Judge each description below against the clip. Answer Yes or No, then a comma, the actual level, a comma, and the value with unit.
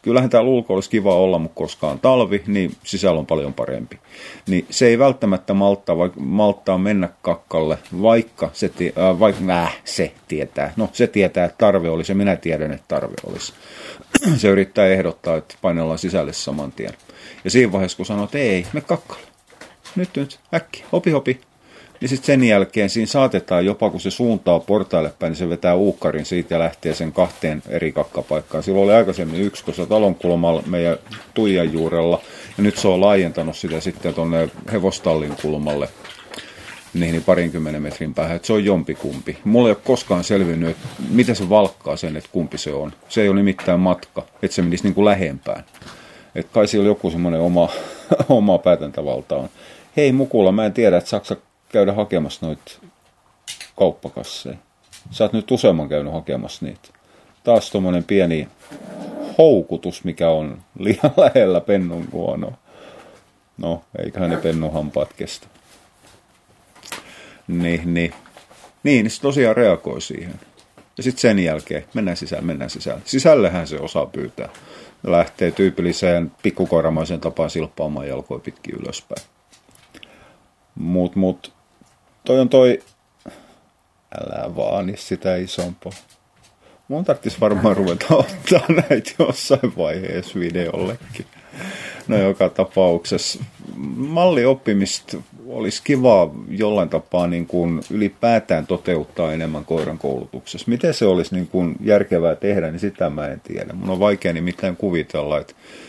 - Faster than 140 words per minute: Yes, average, 150 wpm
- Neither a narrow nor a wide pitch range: Yes, average, 3.9 semitones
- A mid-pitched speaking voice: No, very low, 95 Hz